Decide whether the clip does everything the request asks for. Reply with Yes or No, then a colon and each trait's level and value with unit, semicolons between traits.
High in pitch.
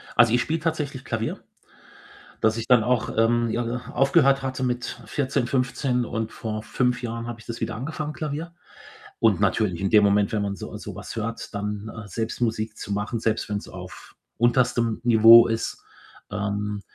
No: low, 115 Hz